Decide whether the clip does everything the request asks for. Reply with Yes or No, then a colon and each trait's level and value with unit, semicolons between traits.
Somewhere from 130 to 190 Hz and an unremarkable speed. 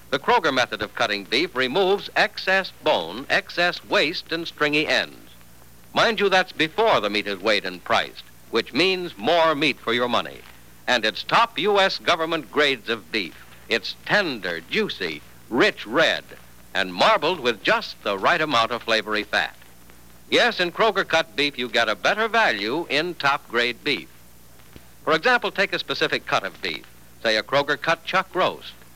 Yes: low, 135 Hz; average, 170 wpm